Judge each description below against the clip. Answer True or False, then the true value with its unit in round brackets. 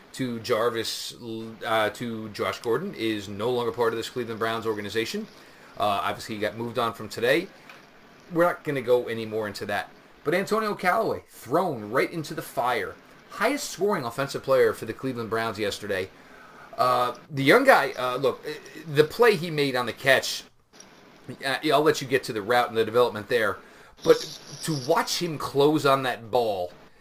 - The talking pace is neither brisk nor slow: True (180 wpm)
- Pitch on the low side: True (125 Hz)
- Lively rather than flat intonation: True (6.5 semitones)